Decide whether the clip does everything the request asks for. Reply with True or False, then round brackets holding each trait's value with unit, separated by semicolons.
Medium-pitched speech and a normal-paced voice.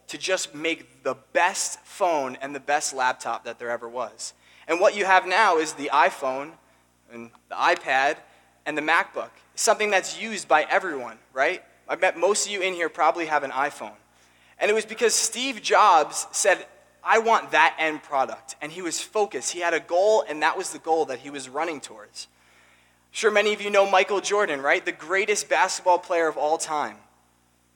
True (160 Hz; 195 wpm)